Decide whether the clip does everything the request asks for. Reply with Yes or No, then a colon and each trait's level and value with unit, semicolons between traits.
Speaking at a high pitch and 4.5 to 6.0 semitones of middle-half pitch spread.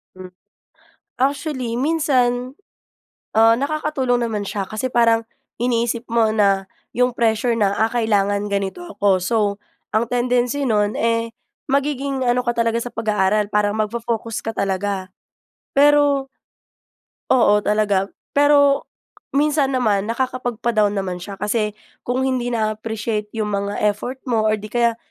No: high, 230 Hz; average, 3.3 semitones